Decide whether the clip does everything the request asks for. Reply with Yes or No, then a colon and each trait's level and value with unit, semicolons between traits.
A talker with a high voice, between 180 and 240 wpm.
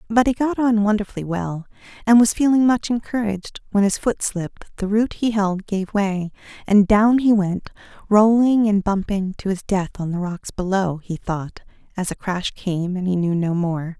Yes: high, 200 Hz; average, 195 wpm